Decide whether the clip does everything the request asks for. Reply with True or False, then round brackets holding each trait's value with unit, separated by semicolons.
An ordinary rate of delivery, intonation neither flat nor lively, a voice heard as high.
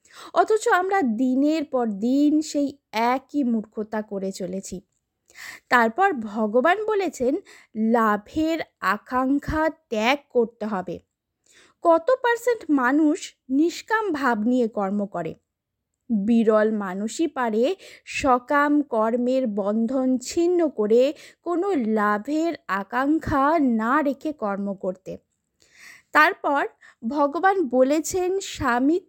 False (95 wpm; 6.4 semitones; 260 Hz)